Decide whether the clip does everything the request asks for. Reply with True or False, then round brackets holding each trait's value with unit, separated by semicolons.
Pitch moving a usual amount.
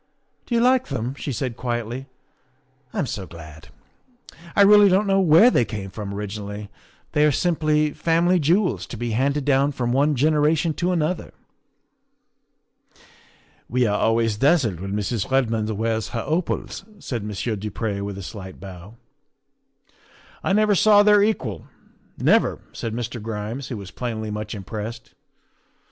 False (6.8 semitones)